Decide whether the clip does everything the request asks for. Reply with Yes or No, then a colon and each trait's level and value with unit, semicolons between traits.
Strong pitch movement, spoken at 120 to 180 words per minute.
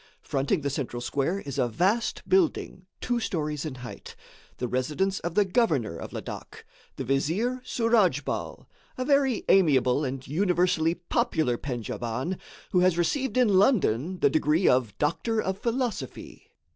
Yes: wide, 7.6 semitones; average, 145 wpm